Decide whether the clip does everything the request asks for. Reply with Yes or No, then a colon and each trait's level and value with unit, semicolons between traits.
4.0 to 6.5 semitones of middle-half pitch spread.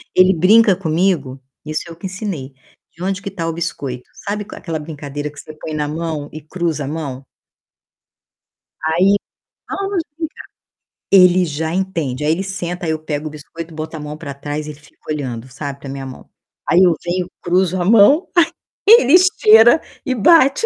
Yes: average, 4.4 semitones